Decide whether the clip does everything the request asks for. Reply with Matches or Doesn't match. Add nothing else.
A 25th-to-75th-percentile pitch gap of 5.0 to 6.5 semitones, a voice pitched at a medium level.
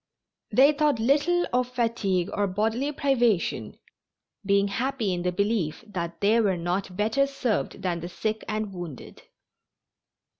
Doesn't match